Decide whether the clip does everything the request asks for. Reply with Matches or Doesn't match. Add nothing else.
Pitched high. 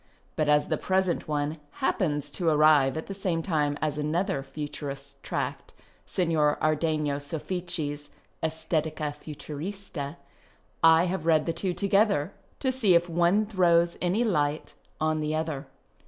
Doesn't match